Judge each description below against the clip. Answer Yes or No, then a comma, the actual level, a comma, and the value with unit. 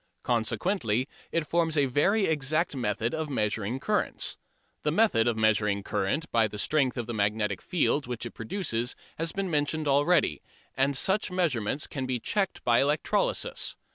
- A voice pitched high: No, low, 135 Hz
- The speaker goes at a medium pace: Yes, average, 160 wpm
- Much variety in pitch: Yes, wide, 6.5 semitones